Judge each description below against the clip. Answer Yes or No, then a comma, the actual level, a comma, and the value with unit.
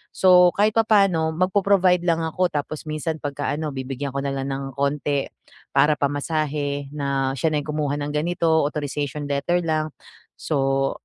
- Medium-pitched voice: Yes, medium, 150 Hz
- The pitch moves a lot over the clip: No, average, 2.8 semitones